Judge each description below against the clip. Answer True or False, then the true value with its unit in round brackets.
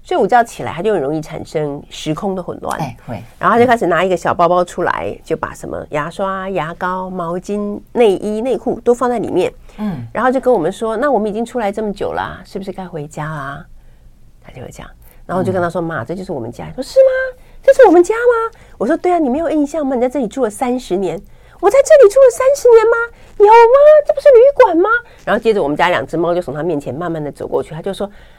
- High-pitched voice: True (205 Hz)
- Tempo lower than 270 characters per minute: False (345 characters per minute)